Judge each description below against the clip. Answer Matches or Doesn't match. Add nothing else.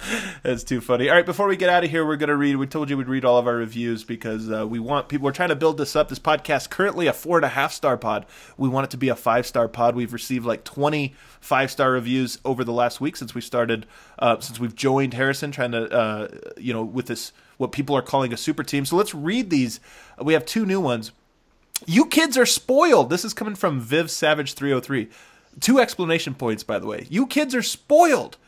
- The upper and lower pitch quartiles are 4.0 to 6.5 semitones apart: Matches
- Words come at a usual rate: Doesn't match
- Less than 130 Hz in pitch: Doesn't match